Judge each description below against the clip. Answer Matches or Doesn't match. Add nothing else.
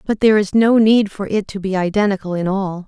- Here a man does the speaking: Doesn't match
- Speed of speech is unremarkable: Doesn't match